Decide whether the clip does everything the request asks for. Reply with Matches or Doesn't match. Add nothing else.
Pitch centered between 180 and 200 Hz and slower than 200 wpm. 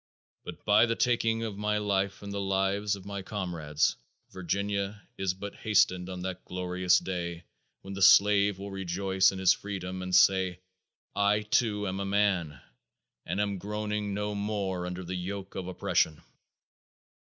Doesn't match